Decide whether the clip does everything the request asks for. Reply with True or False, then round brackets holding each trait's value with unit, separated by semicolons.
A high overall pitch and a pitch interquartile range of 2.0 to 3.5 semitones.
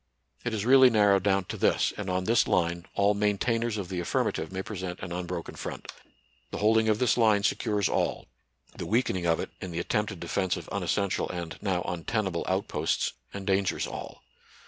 False (100 Hz; 2.9 semitones)